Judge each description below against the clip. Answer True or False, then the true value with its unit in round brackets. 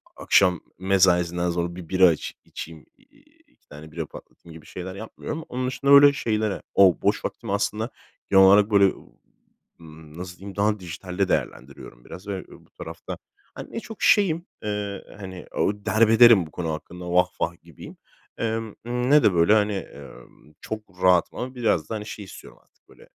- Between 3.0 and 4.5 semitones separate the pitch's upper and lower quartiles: True (3.8 semitones)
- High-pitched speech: False (95 Hz)